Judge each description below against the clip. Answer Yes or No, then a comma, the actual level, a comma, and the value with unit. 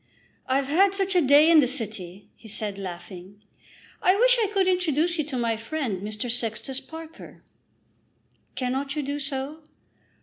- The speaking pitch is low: No, very high, 270 Hz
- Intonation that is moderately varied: No, wide, 6.5 semitones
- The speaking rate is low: No, average, 160 wpm